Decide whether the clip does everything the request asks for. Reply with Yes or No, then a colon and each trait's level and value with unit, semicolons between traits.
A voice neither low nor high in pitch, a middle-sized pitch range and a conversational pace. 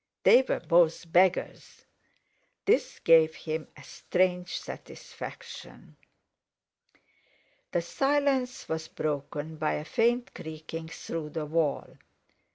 No: medium, 165 Hz; average, 3.0 semitones; slow, 100 wpm